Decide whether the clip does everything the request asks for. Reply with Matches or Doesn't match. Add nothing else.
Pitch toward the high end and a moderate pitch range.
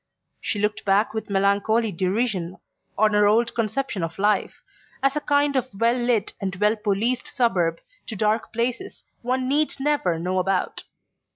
Matches